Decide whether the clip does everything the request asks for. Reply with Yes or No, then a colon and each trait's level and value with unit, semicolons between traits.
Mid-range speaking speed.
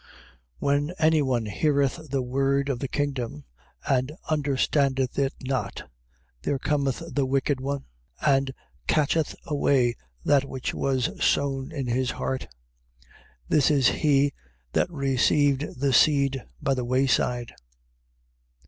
No: slow, 130 wpm